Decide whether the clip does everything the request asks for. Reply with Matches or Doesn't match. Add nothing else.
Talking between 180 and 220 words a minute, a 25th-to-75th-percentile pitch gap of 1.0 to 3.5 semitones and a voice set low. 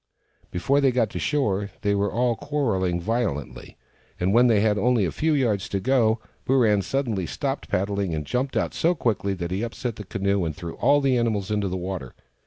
Doesn't match